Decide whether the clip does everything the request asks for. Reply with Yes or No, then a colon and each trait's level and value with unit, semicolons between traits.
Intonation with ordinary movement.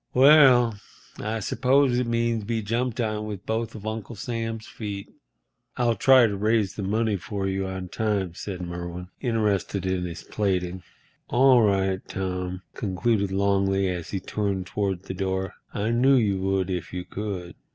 Yes: average, 3.2 semitones